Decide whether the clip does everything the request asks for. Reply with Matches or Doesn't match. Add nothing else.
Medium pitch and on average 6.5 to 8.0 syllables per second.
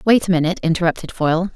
Matches